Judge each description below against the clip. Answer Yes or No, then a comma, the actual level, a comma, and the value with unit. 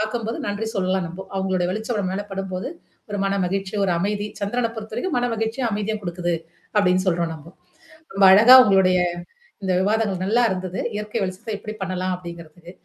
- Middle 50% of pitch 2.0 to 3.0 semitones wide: Yes, average, 2.7 semitones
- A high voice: Yes, high, 195 Hz